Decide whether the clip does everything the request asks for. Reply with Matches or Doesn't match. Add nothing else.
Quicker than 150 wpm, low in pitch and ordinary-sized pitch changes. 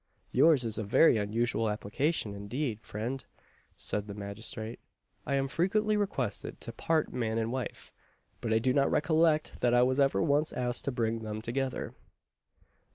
Matches